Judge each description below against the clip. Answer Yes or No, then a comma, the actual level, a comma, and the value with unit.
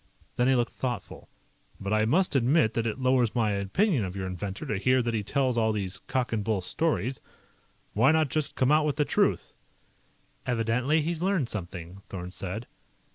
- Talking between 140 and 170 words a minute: No, average, 185 wpm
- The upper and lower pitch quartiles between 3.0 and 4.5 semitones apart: No, average, 5.1 semitones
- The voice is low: Yes, low, 120 Hz